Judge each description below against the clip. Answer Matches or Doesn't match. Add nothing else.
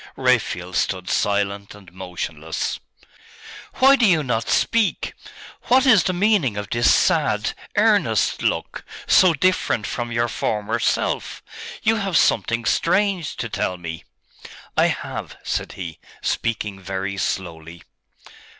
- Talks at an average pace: Doesn't match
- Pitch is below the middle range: Matches